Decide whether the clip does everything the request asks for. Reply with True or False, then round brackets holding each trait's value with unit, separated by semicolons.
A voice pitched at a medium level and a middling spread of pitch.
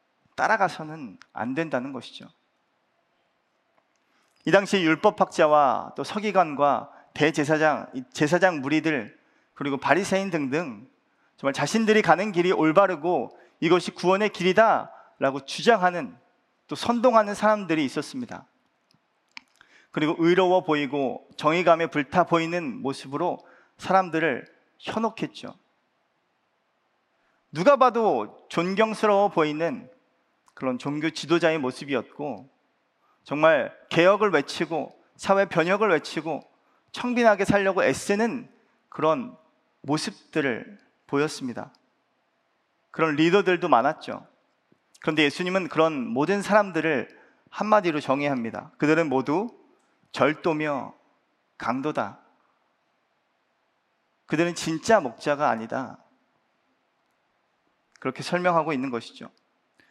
True (170 Hz; 5.0 semitones)